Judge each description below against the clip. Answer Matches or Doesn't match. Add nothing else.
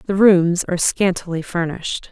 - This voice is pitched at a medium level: Matches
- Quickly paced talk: Doesn't match